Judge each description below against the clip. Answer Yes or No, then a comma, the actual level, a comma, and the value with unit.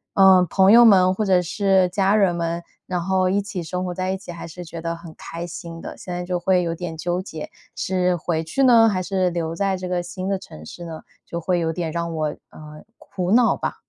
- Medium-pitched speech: Yes, medium, 180 Hz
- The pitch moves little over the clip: Yes, narrow, 2.1 semitones